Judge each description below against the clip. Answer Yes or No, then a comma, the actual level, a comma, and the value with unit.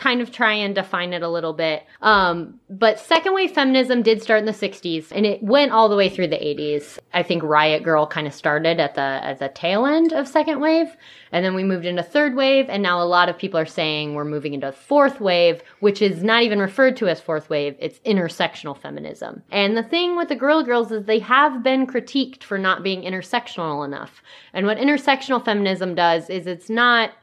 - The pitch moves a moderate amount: No, wide, 6.5 semitones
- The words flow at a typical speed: No, fast, 225 wpm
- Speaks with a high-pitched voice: Yes, high, 200 Hz